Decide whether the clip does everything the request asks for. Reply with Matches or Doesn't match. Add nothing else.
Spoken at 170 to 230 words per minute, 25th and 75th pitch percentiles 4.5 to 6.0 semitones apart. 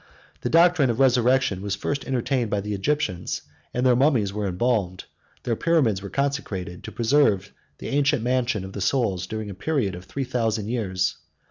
Matches